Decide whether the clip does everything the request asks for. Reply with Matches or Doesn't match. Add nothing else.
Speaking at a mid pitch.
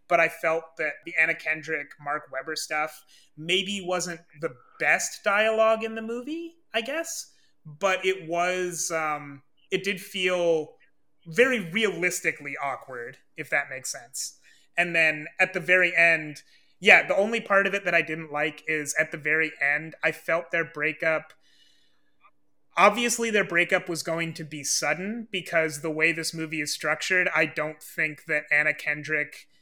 Matches